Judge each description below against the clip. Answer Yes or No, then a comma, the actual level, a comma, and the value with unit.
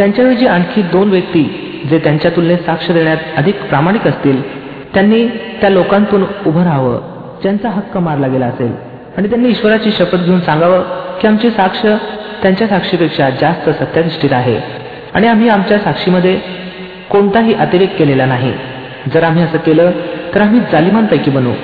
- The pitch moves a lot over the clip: No, average, 4.3 semitones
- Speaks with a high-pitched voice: No, medium, 180 Hz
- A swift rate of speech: Yes, fast, 145 wpm